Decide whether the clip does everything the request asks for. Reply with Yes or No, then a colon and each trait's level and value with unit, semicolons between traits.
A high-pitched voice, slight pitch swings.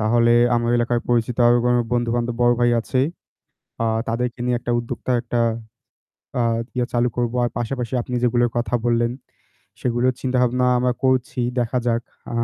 No: low, 120 Hz; narrow, 0.9 semitones